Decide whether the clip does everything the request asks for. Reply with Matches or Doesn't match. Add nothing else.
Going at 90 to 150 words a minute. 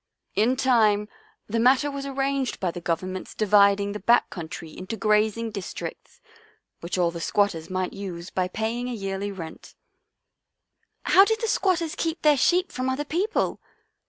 Doesn't match